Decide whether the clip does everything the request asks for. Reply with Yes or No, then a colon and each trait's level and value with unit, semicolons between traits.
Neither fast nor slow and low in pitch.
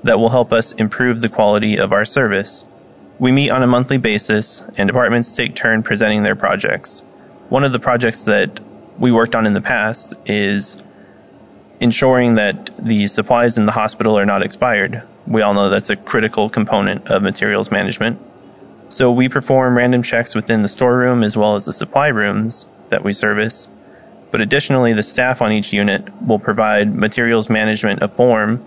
Yes: average, 180 wpm; low, 110 Hz